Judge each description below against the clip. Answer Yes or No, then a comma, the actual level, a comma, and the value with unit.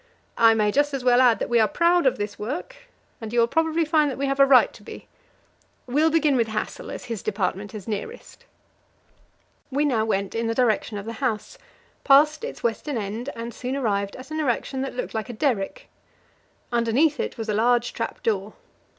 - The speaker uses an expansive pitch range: No, average, 4.3 semitones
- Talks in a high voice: Yes, high, 240 Hz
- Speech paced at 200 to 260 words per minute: Yes, fast, 205 wpm